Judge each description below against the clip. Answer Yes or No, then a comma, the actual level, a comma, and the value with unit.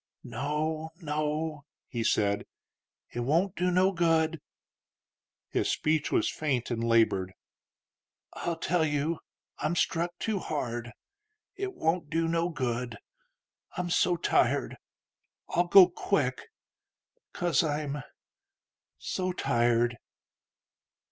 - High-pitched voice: No, medium, 155 Hz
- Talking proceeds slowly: Yes, slow, 105 wpm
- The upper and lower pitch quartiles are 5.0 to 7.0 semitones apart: Yes, average, 5.3 semitones